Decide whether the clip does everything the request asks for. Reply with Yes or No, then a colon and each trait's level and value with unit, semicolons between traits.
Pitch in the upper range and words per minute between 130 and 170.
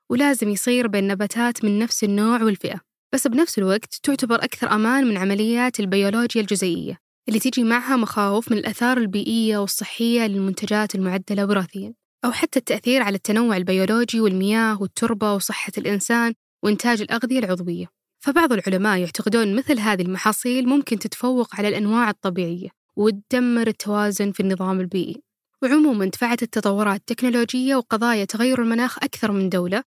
Yes: high, 220 Hz; fast, 135 wpm